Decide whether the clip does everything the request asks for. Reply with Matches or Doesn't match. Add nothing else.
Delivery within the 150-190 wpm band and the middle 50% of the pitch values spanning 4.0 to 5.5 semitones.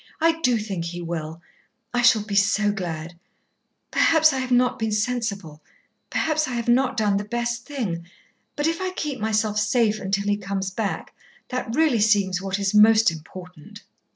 Matches